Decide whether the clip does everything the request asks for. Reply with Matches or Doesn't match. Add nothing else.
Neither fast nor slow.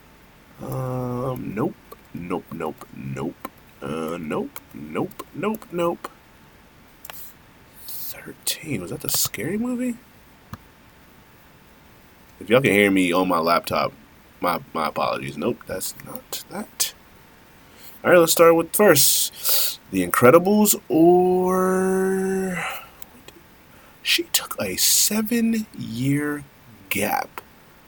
Doesn't match